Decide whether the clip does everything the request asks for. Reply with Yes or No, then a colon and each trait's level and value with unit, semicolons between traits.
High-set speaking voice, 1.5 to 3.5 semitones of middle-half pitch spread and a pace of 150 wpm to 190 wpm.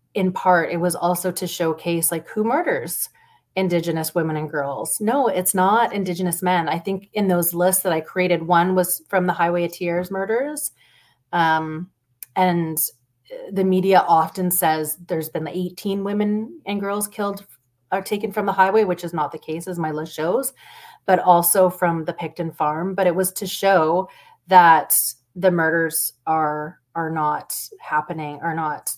No: medium, 180 Hz; average, 3.0 semitones; average, 170 wpm